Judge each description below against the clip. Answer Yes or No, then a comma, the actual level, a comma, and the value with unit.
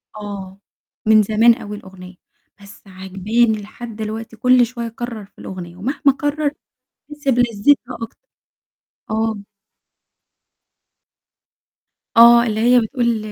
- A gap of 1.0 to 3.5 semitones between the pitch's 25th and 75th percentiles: Yes, average, 2.8 semitones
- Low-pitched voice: No, high, 225 Hz